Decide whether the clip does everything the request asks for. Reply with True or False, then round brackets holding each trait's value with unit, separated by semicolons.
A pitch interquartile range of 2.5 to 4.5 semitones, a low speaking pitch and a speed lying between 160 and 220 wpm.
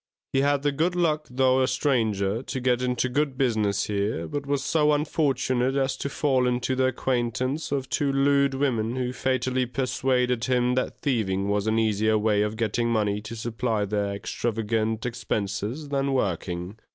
True (3.6 semitones; 125 Hz; 170 wpm)